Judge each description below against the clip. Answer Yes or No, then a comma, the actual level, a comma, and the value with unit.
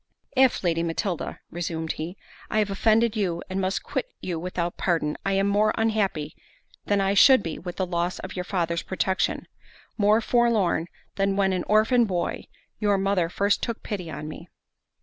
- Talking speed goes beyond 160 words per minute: Yes, average, 170 wpm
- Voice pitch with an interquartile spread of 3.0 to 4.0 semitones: Yes, average, 3.4 semitones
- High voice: Yes, high, 195 Hz